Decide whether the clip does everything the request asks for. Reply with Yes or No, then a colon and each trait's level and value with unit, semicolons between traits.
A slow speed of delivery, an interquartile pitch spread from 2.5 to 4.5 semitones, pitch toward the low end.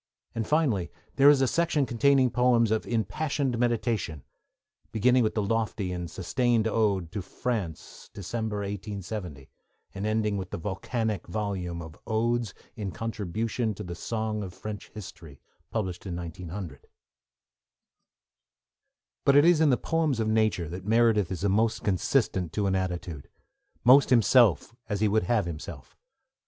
No: average, 145 wpm; average, 4.1 semitones; low, 105 Hz